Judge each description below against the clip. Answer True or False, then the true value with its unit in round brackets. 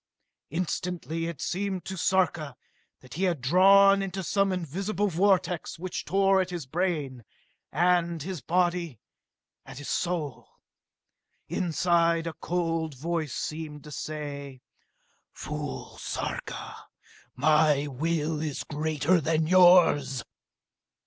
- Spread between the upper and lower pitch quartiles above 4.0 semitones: False (3.4 semitones)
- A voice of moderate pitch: True (165 Hz)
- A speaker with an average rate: False (115 wpm)